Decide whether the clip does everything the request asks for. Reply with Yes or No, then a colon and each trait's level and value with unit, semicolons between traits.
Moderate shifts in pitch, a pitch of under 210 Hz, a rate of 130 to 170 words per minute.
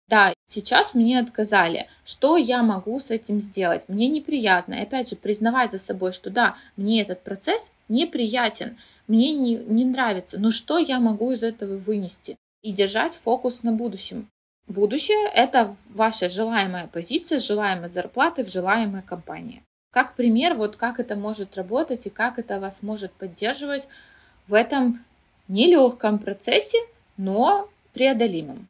No: average, 4.0 semitones; high, 230 Hz; average, 145 wpm